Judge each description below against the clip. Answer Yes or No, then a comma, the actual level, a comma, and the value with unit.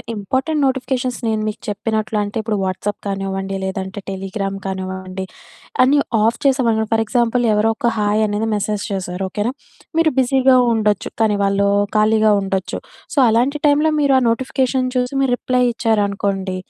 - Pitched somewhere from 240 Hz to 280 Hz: No, high, 215 Hz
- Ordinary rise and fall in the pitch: Yes, average, 4.2 semitones